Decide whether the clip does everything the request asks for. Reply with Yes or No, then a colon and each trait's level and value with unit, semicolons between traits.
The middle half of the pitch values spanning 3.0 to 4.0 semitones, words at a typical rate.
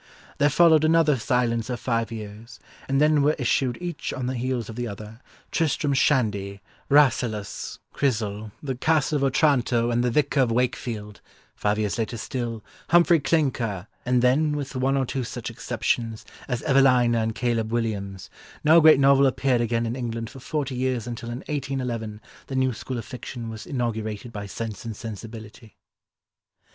Yes: average, 3.3 semitones; average, 160 wpm